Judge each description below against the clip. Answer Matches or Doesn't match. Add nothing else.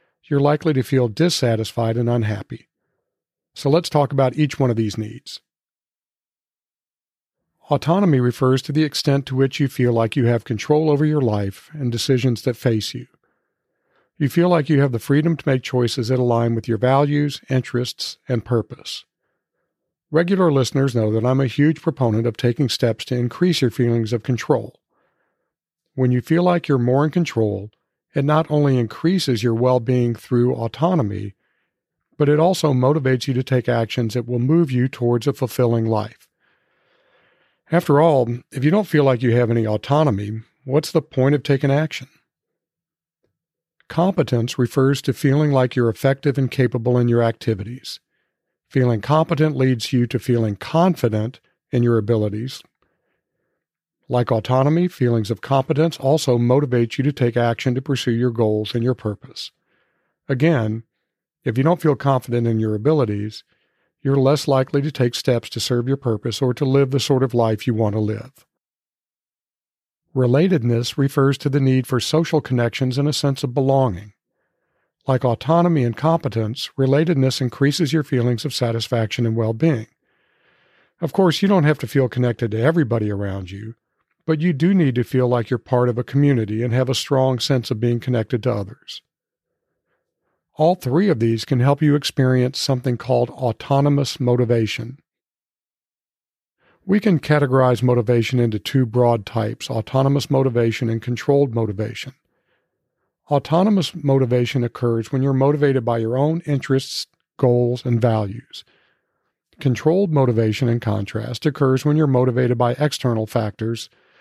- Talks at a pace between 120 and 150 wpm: Doesn't match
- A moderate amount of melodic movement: Matches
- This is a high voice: Doesn't match